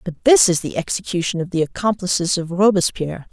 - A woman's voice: Yes, female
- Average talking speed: Yes, average, 180 wpm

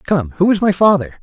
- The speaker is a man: Yes, male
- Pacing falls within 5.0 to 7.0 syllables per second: Yes, 5.8 syllables/s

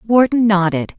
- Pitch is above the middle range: Yes, high, 205 Hz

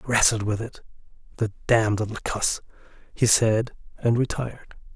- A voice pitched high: No, low, 110 Hz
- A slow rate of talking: Yes, slow, 120 wpm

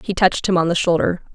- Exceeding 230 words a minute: Yes, fast, 270 wpm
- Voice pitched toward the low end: No, medium, 175 Hz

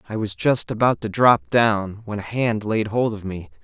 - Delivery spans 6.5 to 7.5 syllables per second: No, 4.6 syllables/s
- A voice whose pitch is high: No, low, 105 Hz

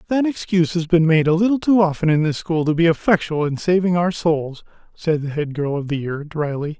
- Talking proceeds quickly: Yes, fast, 240 wpm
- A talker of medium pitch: Yes, medium, 165 Hz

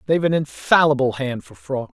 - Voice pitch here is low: No, medium, 145 Hz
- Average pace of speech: Yes, average, 180 wpm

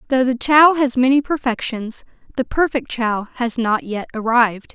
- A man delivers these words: No, female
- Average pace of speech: Yes, average, 165 wpm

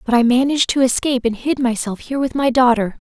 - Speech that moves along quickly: Yes, fast, 235 wpm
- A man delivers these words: No, female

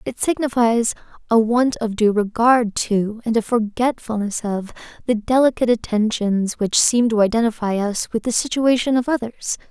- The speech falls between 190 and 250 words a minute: No, average, 155 wpm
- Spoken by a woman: Yes, female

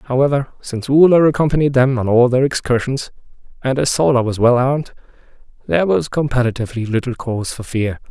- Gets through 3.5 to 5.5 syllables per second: No, 6.2 syllables/s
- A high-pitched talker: No, low, 130 Hz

